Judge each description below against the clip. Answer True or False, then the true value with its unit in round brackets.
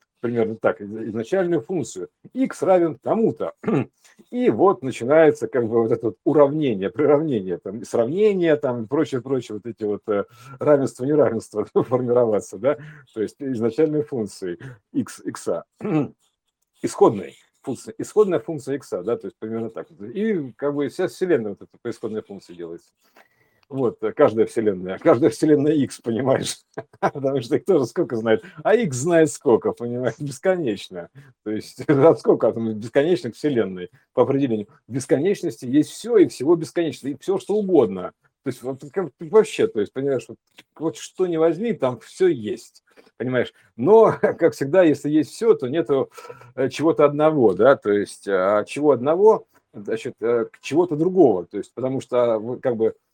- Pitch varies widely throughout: True (6.7 semitones)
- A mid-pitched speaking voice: True (145 Hz)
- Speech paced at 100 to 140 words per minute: False (155 wpm)